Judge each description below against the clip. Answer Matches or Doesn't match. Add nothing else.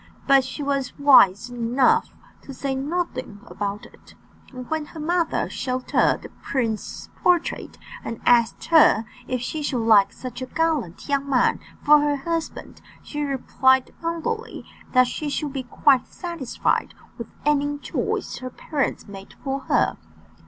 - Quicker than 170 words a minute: Doesn't match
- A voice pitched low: Doesn't match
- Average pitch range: Matches